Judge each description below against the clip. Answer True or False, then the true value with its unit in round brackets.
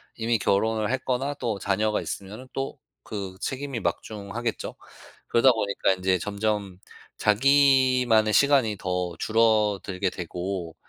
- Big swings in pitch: False (4.1 semitones)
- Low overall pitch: True (110 Hz)